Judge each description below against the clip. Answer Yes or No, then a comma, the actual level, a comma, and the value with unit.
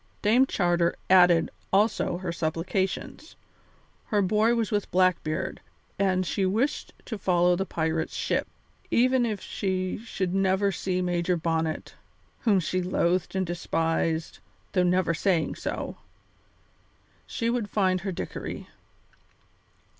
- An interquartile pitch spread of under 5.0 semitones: Yes, average, 2.8 semitones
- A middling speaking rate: No, slow, 125 wpm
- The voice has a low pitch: No, medium, 185 Hz